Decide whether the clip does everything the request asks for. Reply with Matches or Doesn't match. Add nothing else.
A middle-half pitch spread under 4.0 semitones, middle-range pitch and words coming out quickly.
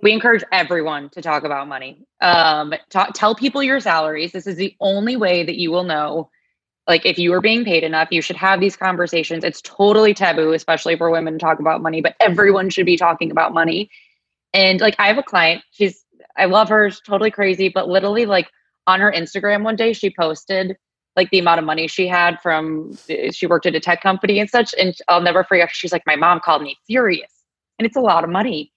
Matches